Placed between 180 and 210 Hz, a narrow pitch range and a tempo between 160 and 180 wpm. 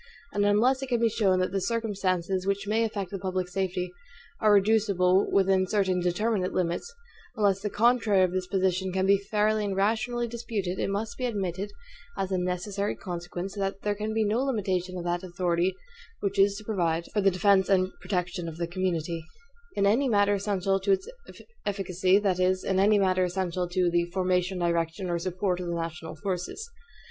No: high, 190 Hz; narrow, 2.3 semitones; average, 190 wpm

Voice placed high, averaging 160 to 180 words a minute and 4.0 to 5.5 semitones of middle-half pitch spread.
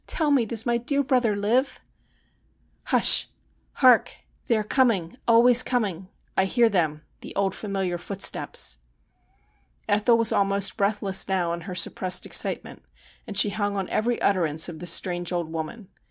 Yes: high, 200 Hz; average, 170 wpm; average, 4.5 semitones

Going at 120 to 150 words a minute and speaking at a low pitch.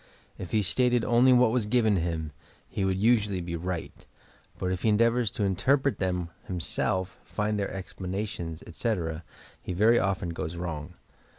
No: average, 160 wpm; very low, 95 Hz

